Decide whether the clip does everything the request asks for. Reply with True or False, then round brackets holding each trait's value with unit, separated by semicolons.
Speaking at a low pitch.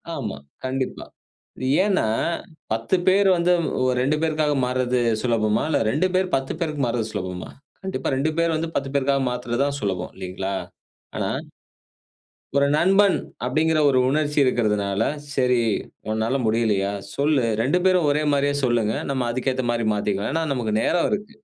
True (130 Hz)